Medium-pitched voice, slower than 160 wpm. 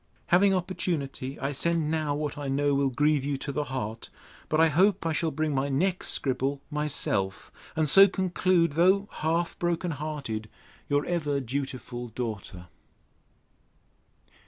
Yes: medium, 150 Hz; average, 145 wpm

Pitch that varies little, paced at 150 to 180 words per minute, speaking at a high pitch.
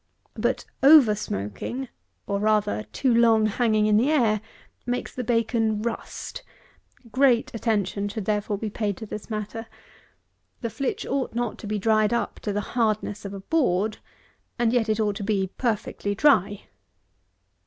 Yes: narrow, 2.3 semitones; average, 155 wpm; high, 215 Hz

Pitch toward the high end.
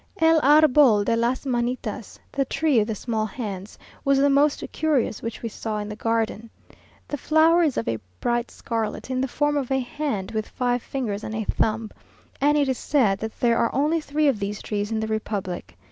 Yes: high, 235 Hz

